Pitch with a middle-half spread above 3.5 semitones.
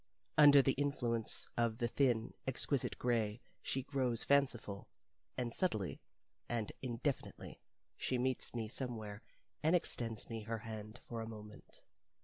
No: average, 3.0 semitones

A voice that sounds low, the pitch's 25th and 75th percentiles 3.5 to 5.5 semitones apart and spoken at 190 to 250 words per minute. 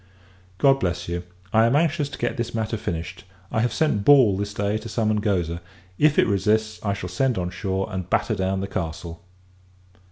Yes: low, 105 Hz; average, 3.9 semitones; average, 195 wpm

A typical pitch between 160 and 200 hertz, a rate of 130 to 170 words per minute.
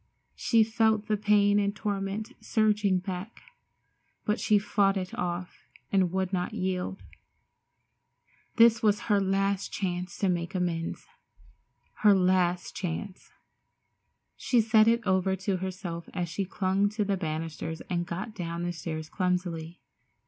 Yes: high, 190 Hz; slow, 135 wpm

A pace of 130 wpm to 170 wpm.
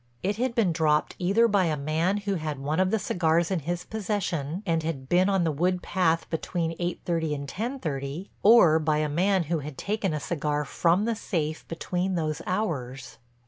No: average, 200 wpm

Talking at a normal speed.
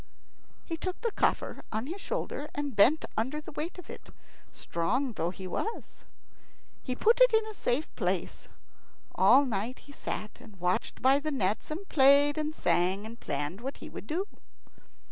Yes: average, 175 wpm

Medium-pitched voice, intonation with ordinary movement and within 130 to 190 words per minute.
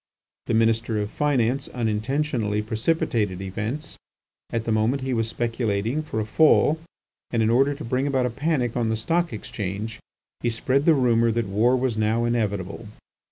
No: low, 115 Hz; average, 3.3 semitones; average, 165 wpm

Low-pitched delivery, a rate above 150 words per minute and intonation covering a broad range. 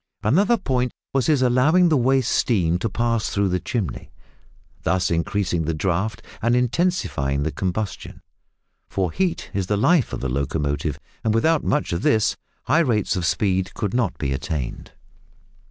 Yes: low, 105 Hz; average, 160 wpm; wide, 6.9 semitones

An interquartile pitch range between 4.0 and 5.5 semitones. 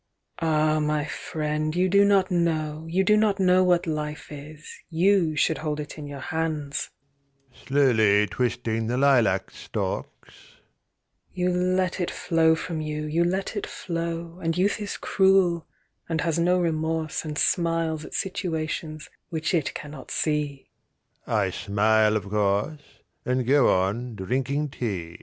No: average, 3.5 semitones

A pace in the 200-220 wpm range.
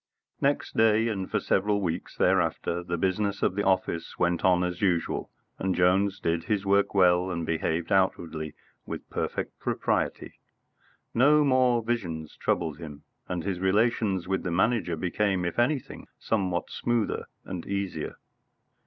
No: average, 150 wpm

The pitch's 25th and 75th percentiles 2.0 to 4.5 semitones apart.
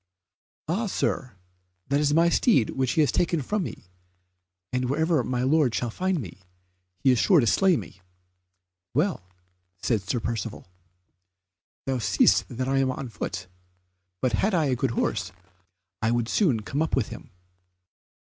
No: wide, 5.4 semitones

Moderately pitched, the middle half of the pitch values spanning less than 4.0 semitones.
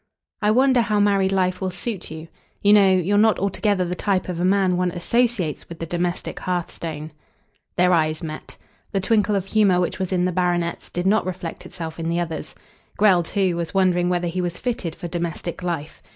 Yes: medium, 180 Hz; narrow, 2.5 semitones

